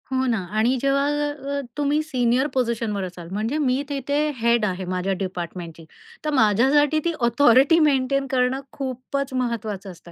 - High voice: Yes, very high, 255 Hz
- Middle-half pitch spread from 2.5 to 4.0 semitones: No, average, 4.7 semitones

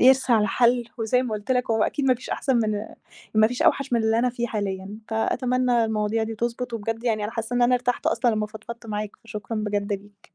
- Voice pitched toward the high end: Yes, high, 225 Hz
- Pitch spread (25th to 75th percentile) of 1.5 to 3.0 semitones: Yes, narrow, 2.5 semitones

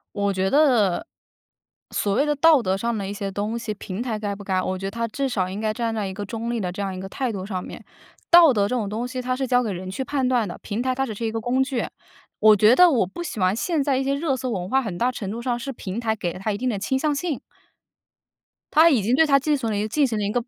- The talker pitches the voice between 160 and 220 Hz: No, high, 230 Hz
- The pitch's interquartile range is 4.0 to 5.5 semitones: Yes, average, 4.6 semitones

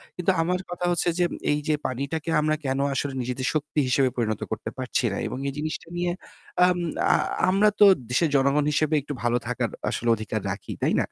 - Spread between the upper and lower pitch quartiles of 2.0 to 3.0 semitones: No, average, 4.5 semitones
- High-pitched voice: No, medium, 145 Hz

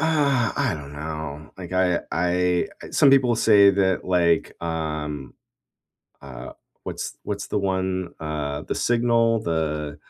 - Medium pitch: No, very low, 90 Hz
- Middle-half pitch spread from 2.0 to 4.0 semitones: No, average, 5.2 semitones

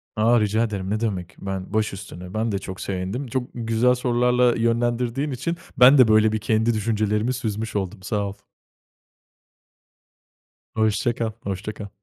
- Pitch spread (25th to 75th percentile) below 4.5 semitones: Yes, average, 2.9 semitones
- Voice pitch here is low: Yes, low, 110 Hz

